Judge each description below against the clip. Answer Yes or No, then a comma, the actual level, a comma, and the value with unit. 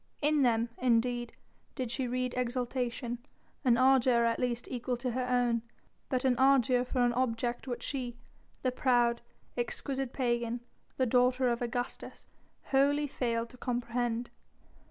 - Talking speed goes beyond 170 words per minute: No, average, 140 wpm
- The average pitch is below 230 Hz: No, high, 245 Hz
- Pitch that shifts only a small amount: Yes, narrow, 1.3 semitones